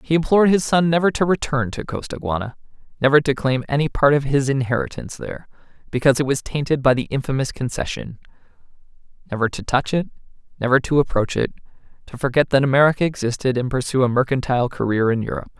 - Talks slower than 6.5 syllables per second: No, 6.7 syllables/s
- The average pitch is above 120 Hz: Yes, low, 135 Hz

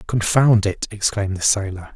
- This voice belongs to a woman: No, male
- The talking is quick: No, average, 155 wpm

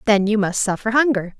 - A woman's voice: Yes, female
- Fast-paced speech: Yes, fast, 215 wpm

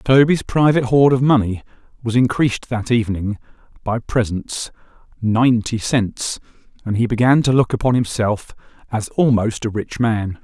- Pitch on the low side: Yes, low, 115 Hz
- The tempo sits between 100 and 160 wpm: Yes, average, 145 wpm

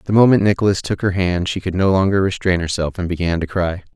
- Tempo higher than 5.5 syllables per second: Yes, 6.2 syllables/s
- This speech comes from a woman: No, male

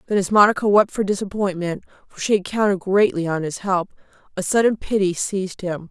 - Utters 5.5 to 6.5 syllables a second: Yes, 5.8 syllables/s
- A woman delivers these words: Yes, female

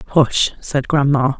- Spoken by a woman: Yes, female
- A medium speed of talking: No, slow, 130 wpm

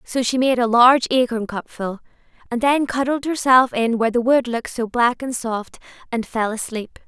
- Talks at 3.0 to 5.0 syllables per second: Yes, 4.9 syllables/s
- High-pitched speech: Yes, high, 240 Hz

